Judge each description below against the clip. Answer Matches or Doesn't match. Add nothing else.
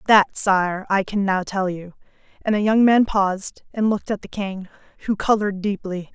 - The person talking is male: Doesn't match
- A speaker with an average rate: Matches